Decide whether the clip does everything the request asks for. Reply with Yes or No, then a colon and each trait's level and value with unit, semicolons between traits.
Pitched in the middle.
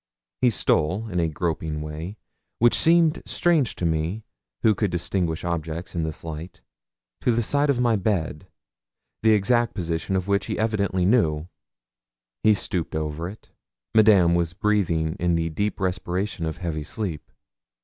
No: very low, 90 Hz